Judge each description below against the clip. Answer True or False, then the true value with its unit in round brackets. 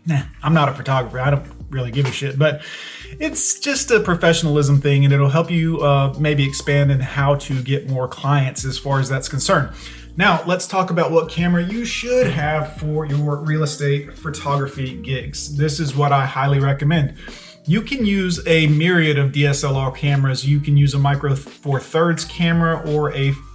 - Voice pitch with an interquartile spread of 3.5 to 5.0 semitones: False (2.9 semitones)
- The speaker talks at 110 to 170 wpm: False (190 wpm)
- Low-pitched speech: False (145 Hz)